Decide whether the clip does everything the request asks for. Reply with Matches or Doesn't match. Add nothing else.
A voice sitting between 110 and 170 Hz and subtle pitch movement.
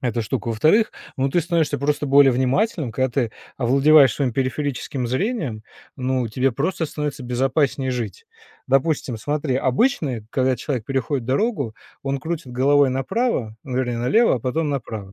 Doesn't match